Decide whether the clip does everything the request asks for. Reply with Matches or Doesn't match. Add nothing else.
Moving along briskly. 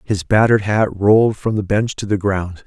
Matches